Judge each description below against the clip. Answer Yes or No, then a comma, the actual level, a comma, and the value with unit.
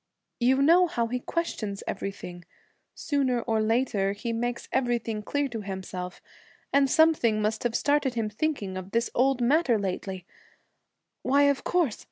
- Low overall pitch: No, high, 235 Hz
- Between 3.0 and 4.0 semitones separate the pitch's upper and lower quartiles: No, average, 4.6 semitones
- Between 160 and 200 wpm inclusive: No, average, 150 wpm